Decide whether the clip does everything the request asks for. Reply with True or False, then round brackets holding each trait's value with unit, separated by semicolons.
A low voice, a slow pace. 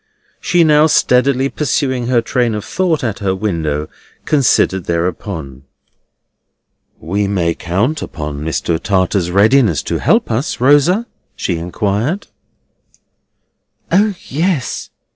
True (110 Hz; 110 wpm)